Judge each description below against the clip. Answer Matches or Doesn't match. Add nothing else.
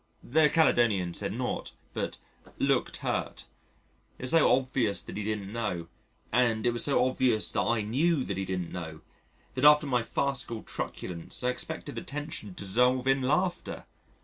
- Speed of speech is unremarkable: Matches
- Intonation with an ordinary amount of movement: Matches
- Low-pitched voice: Matches